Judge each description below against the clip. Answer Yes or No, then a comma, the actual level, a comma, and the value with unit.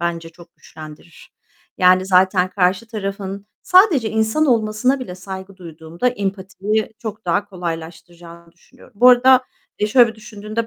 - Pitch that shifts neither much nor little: Yes, average, 4.0 semitones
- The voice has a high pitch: Yes, high, 195 Hz